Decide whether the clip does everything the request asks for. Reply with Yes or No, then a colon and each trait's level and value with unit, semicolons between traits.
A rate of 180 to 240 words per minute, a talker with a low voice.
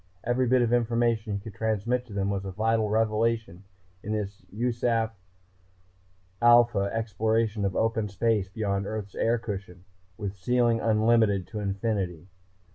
No: average, 140 wpm; low, 110 Hz